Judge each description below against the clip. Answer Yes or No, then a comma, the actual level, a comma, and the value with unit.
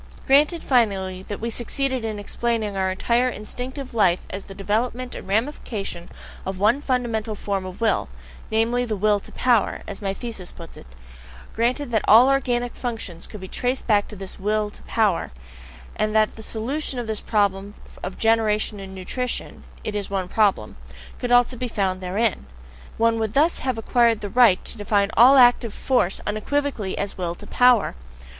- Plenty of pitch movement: No, average, 3.5 semitones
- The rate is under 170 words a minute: No, average, 175 wpm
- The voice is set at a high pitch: Yes, high, 220 Hz